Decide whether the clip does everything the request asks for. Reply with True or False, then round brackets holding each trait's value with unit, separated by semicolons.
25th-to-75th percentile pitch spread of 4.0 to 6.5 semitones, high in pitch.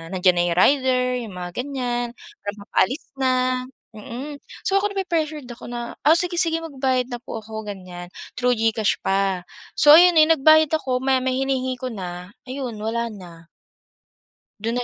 True (5.2 semitones; 250 Hz)